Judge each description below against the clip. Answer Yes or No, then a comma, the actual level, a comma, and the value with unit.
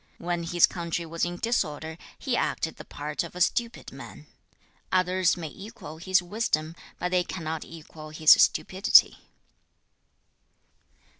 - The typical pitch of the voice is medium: Yes, medium, 175 Hz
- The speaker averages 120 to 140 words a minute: Yes, slow, 135 wpm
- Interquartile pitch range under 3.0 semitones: Yes, narrow, 2.6 semitones